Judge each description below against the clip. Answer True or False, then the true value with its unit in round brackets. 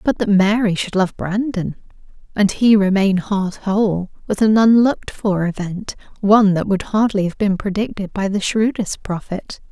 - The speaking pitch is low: False (200 Hz)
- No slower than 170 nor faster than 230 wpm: False (160 wpm)